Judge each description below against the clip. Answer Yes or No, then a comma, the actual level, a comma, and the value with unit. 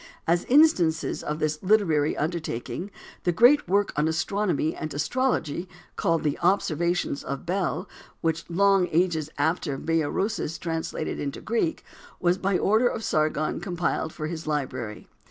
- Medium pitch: Yes, medium, 170 Hz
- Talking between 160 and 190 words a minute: No, slow, 135 wpm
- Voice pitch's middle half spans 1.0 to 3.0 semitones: No, average, 4.1 semitones